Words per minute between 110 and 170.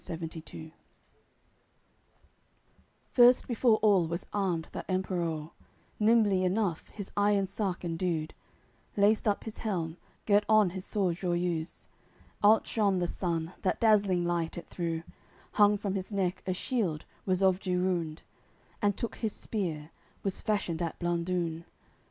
Yes: slow, 135 wpm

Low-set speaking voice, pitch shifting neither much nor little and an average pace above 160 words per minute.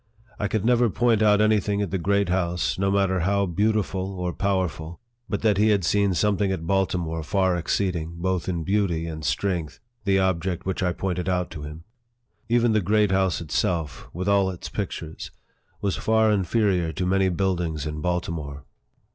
Yes: very low, 95 Hz; average, 3.0 semitones; average, 180 wpm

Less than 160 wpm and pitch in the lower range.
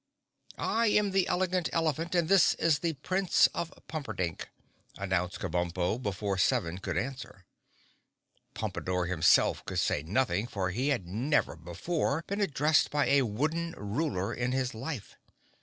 Yes: average, 140 wpm; low, 130 Hz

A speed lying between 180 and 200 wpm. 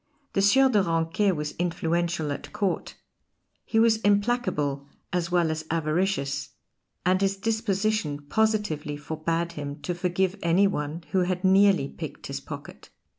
No: average, 140 wpm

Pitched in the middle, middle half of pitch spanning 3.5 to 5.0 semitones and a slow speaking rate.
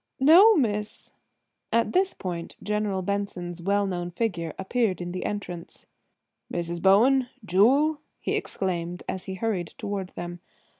No: high, 195 Hz; average, 4.4 semitones; slow, 130 wpm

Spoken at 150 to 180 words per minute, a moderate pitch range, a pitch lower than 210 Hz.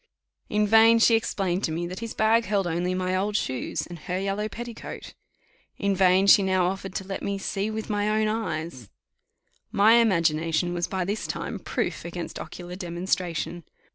Yes: average, 175 wpm; average, 3.3 semitones; high, 190 Hz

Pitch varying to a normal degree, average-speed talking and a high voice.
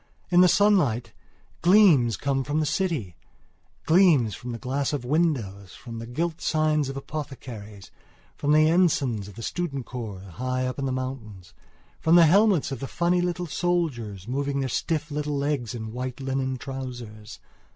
No: average, 5.0 semitones; average, 160 wpm; low, 135 Hz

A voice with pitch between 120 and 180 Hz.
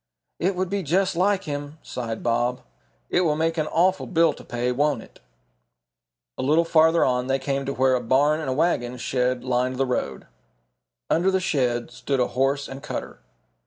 Yes: medium, 140 Hz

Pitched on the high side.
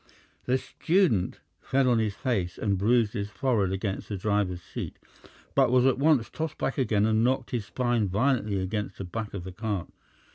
No: low, 110 Hz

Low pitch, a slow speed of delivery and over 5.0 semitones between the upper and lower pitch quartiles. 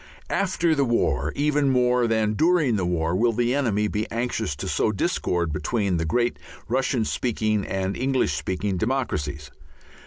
No: low, 115 Hz; average, 155 wpm; wide, 5.6 semitones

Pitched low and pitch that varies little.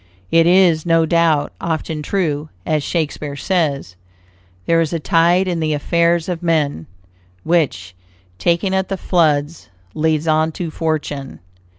No: medium, 160 Hz; narrow, 2.2 semitones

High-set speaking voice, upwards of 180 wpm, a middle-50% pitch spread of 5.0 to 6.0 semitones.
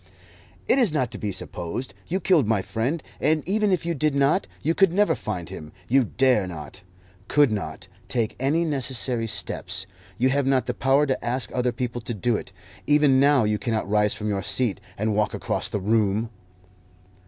No: low, 125 Hz; average, 190 wpm; wide, 5.4 semitones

